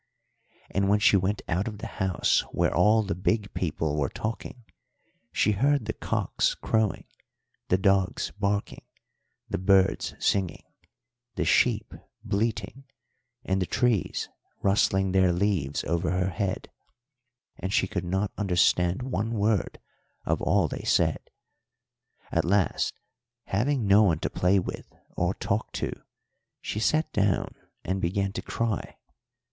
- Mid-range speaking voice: No, low, 100 Hz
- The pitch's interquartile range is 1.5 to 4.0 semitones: Yes, narrow, 2.5 semitones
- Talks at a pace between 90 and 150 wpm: Yes, slow, 135 wpm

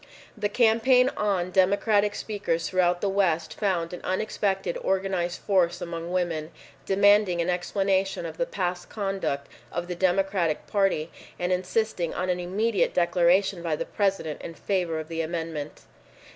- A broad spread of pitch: No, narrow, 2.6 semitones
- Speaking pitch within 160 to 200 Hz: Yes, medium, 185 Hz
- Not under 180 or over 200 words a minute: No, average, 145 wpm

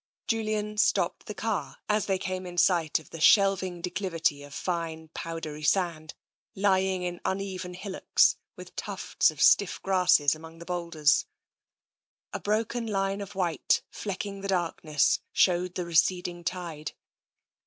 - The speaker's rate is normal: Yes, average, 145 wpm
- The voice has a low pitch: No, medium, 180 Hz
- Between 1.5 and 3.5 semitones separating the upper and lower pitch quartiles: Yes, average, 2.8 semitones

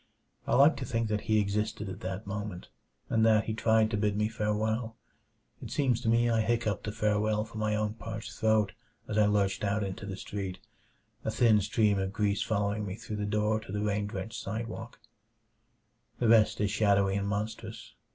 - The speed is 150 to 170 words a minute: No, average, 195 wpm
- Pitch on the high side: No, low, 105 Hz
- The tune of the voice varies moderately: No, narrow, 1.4 semitones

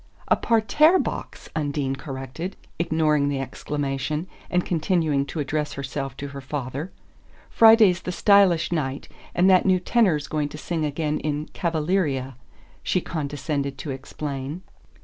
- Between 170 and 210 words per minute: No, slow, 135 wpm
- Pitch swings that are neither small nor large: Yes, average, 4.1 semitones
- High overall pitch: No, medium, 150 Hz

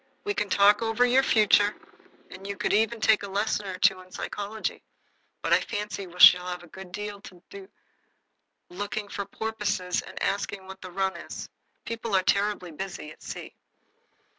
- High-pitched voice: Yes, high, 200 Hz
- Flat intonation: Yes, narrow, 2.1 semitones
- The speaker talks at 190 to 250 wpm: No, average, 180 wpm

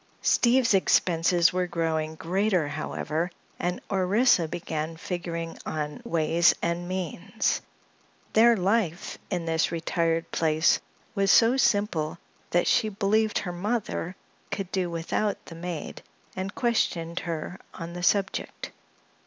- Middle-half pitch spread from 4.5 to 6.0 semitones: No, average, 3.1 semitones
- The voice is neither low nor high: Yes, medium, 175 Hz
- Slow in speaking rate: Yes, slow, 120 wpm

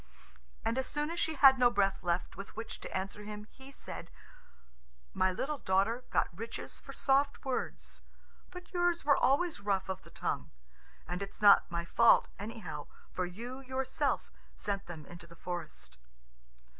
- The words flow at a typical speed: Yes, average, 165 wpm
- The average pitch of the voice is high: Yes, high, 220 Hz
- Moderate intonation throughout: No, wide, 6.1 semitones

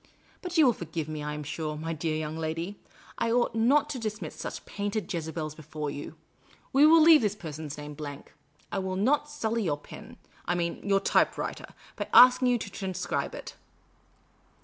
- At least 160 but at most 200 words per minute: Yes, average, 195 wpm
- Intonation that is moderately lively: No, wide, 7.1 semitones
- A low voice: No, medium, 185 Hz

